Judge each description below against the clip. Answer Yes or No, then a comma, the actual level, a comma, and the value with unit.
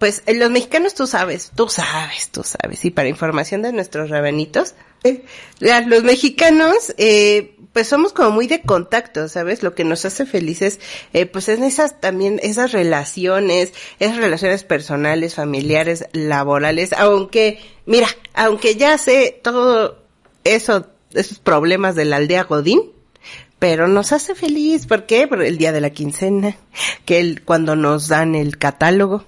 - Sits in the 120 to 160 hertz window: No, high, 195 Hz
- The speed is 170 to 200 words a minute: No, average, 160 wpm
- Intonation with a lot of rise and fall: Yes, wide, 6.2 semitones